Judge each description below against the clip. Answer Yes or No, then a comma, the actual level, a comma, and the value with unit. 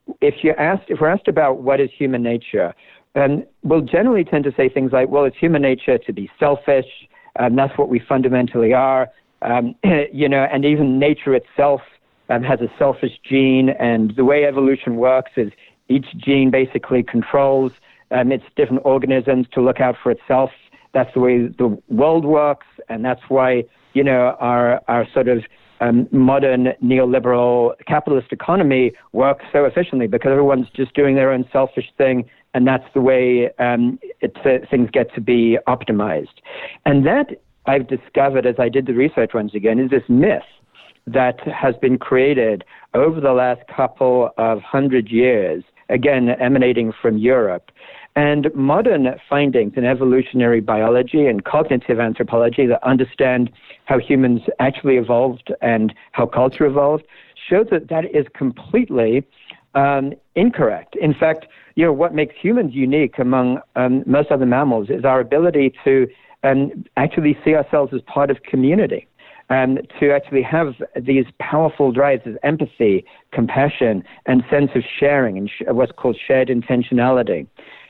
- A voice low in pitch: Yes, low, 130 Hz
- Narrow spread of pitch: Yes, narrow, 2.1 semitones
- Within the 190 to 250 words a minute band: No, average, 160 wpm